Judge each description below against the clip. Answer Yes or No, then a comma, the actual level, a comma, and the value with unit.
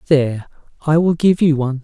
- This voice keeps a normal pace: Yes, average, 195 wpm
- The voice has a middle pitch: Yes, medium, 150 Hz